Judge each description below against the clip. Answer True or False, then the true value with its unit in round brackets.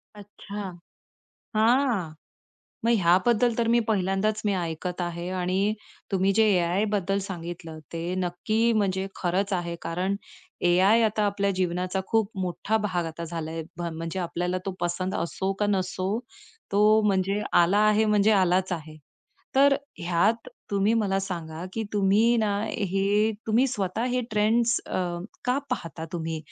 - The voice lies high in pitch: True (195 Hz)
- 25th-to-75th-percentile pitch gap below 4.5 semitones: True (3.3 semitones)